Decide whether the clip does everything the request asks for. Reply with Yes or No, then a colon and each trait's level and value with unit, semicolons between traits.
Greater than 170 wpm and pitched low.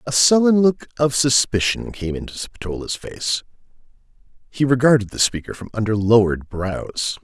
No: average, 140 wpm; low, 120 Hz